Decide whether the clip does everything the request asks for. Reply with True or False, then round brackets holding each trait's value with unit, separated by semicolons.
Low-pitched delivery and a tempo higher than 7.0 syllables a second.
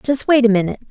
False (240 Hz; 8.1 syllables/s)